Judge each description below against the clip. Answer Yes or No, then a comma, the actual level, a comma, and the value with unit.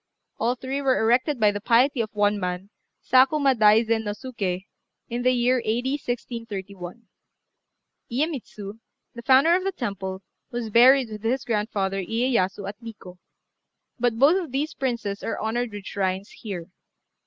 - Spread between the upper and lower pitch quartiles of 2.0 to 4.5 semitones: Yes, average, 4.0 semitones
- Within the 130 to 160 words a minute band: Yes, average, 150 wpm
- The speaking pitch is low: No, high, 230 Hz